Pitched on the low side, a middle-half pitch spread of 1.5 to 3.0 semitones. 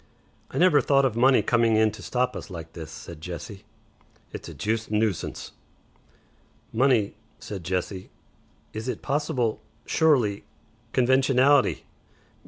No: low, 115 Hz; average, 4.8 semitones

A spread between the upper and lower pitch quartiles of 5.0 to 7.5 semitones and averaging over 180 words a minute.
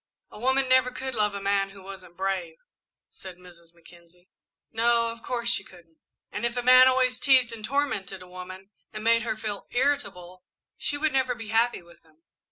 Yes: wide, 5.4 semitones; average, 190 wpm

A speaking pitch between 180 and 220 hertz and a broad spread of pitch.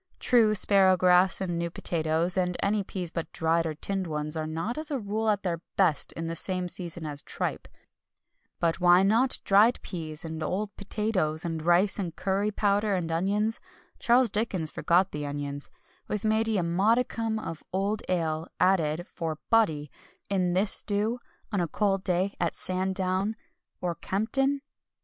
No: medium, 185 Hz; average, 3.9 semitones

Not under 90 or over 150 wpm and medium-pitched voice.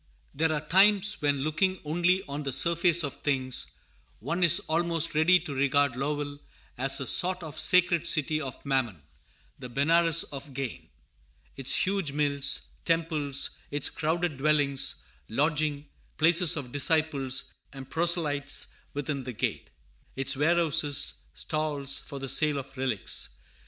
Yes: average, 140 wpm; medium, 150 Hz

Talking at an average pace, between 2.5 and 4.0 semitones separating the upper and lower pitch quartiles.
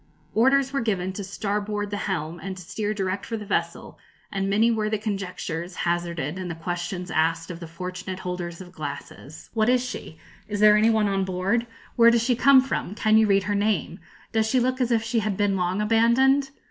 No: fast, 210 wpm; average, 3.7 semitones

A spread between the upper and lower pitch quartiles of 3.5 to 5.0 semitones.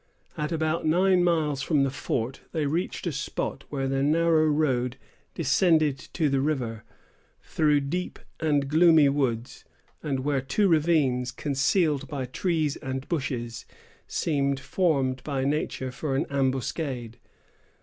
No: average, 3.1 semitones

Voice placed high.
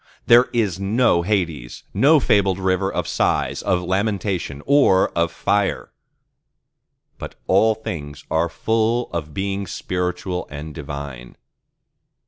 No: very low, 95 Hz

